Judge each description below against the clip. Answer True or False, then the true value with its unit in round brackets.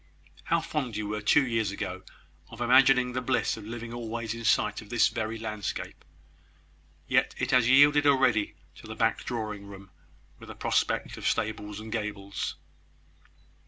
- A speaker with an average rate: True (160 wpm)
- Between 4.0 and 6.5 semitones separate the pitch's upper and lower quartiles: False (2.9 semitones)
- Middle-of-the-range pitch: False (115 Hz)